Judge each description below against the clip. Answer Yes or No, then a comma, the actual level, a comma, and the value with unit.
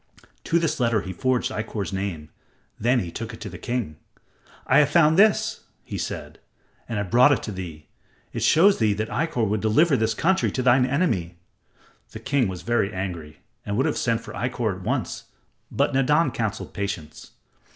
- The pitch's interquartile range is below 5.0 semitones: No, average, 5.3 semitones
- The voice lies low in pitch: Yes, low, 115 Hz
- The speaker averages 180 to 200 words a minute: Yes, average, 185 wpm